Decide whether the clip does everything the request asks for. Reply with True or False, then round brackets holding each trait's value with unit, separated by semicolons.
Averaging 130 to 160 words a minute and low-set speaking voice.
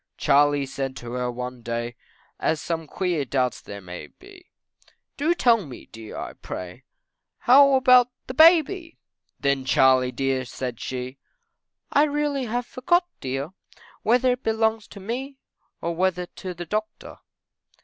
False (145 wpm; 175 Hz)